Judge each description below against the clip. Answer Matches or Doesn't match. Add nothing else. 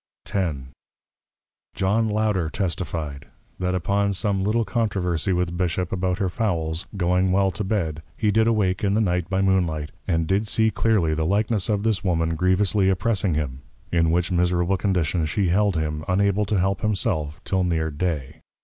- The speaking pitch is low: Matches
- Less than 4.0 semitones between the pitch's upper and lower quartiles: Matches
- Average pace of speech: Matches